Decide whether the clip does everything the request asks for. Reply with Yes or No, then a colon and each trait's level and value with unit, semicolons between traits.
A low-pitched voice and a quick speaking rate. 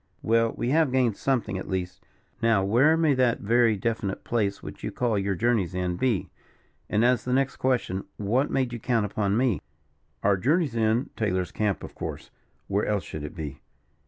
No: low, 110 Hz; average, 190 wpm